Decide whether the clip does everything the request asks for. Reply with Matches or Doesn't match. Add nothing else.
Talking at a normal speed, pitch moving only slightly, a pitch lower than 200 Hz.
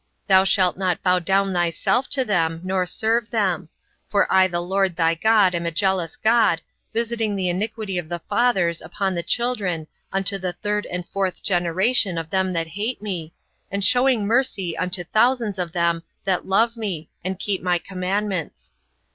Doesn't match